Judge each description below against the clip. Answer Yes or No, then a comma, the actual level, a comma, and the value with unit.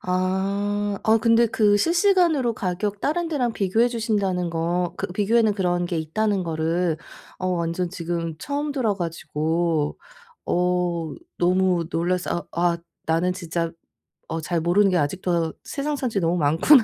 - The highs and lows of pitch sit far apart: No, average, 4.2 semitones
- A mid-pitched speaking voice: Yes, medium, 180 Hz